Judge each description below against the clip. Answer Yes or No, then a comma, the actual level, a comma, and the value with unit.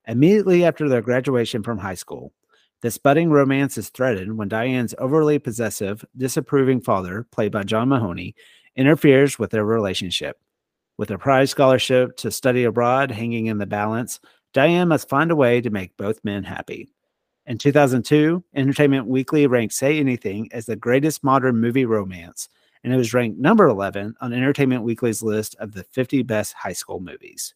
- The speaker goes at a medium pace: Yes, average, 170 wpm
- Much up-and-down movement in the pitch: No, average, 4.1 semitones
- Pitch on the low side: Yes, low, 125 Hz